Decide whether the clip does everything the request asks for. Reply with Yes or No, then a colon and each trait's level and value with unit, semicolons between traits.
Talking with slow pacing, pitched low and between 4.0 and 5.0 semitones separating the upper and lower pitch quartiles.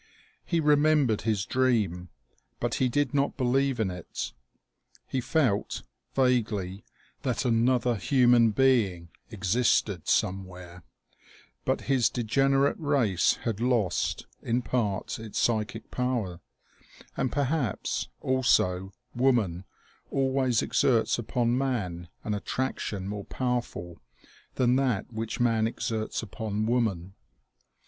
Yes: slow, 110 wpm; low, 115 Hz; average, 4.4 semitones